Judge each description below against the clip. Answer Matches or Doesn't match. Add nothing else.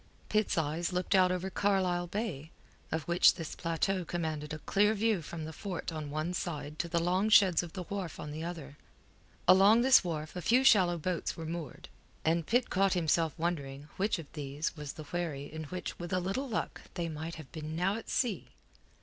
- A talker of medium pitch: Matches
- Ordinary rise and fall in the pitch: Matches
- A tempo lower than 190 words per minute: Doesn't match